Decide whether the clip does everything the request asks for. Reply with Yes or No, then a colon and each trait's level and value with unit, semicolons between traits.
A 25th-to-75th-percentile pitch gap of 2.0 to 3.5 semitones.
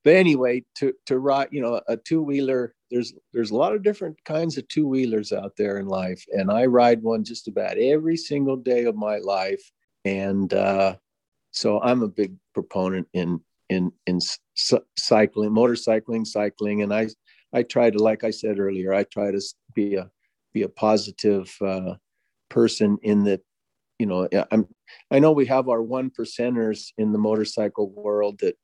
No: average, 4.3 semitones